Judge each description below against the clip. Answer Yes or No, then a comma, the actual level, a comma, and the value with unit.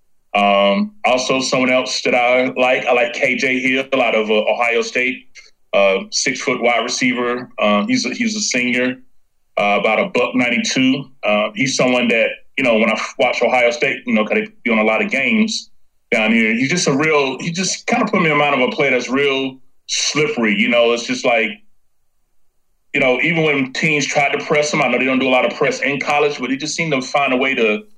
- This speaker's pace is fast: Yes, fast, 230 wpm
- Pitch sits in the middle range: No, low, 130 Hz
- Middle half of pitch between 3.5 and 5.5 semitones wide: Yes, average, 3.8 semitones